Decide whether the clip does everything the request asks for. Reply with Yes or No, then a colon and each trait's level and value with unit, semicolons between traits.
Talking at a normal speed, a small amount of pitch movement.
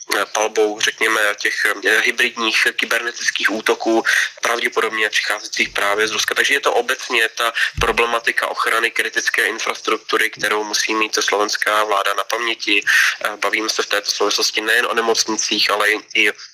Yes: average, 135 wpm; narrow, 1.1 semitones